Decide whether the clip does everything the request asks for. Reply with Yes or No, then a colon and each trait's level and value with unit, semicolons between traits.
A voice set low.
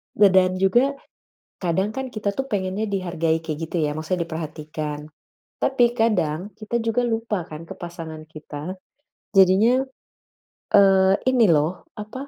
No: high, 190 Hz